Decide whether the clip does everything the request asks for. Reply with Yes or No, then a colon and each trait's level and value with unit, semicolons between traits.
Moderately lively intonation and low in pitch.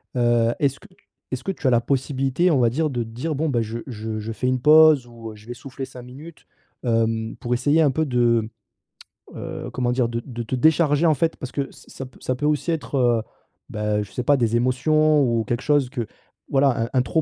Yes: average, 3.7 semitones; low, 125 Hz